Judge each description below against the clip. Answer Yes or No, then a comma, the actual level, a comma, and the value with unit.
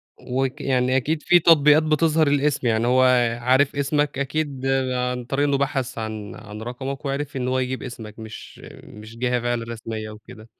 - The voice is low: Yes, low, 130 Hz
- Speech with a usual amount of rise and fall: Yes, average, 3.3 semitones